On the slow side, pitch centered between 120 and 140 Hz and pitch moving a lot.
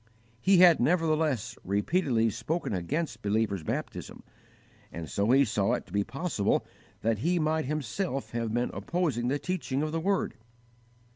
No: average, 150 wpm; low, 135 Hz; wide, 6.5 semitones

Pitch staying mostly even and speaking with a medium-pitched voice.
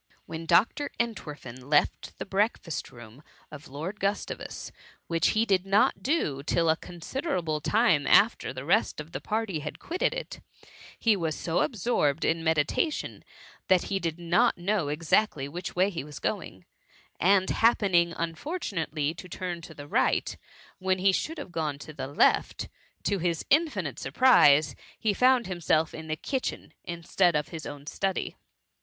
No: average, 4.9 semitones; medium, 175 Hz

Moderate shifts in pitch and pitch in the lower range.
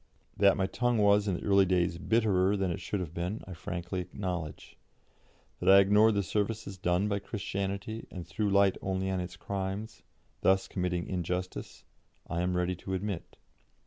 No: narrow, 2.2 semitones; very low, 95 Hz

